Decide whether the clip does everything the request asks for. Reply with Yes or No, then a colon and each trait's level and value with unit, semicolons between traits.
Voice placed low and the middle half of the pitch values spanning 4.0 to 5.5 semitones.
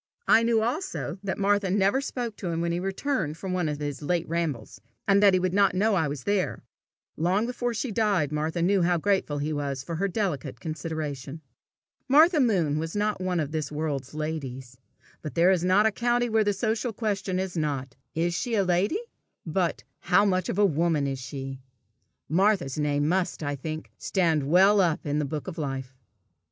No: medium, 175 Hz; average, 5.2 semitones